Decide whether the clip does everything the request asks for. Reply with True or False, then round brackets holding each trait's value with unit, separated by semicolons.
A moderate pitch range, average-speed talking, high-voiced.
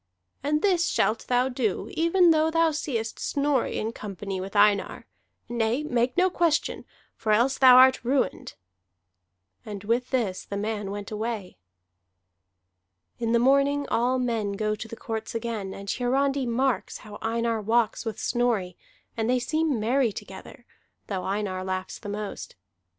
True (4.0 semitones; 150 wpm; 235 Hz)